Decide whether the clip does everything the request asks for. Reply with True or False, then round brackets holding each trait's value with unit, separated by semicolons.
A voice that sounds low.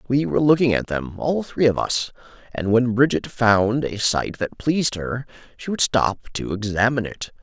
True (120 Hz)